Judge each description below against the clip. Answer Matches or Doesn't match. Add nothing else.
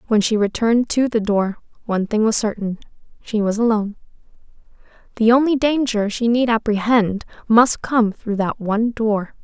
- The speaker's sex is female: Matches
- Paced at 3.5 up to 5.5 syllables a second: Matches